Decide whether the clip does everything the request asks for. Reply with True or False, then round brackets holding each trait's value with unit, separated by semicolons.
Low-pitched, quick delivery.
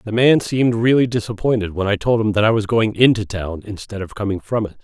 True (105 Hz; 250 wpm)